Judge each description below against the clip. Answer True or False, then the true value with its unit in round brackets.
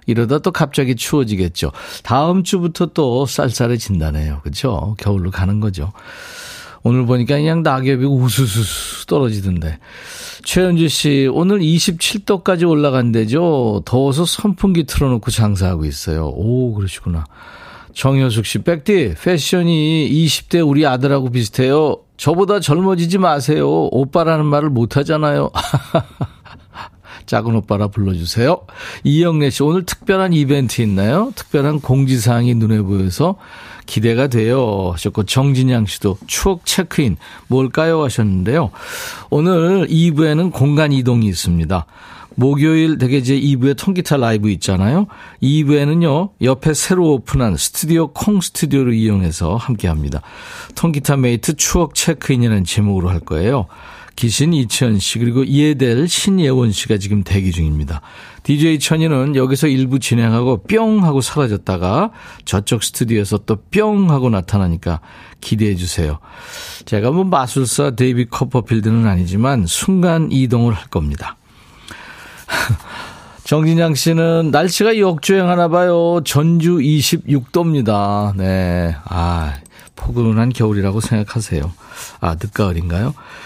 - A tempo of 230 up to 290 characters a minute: False (300 characters per minute)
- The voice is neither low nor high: False (130 Hz)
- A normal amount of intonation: False (7.2 semitones)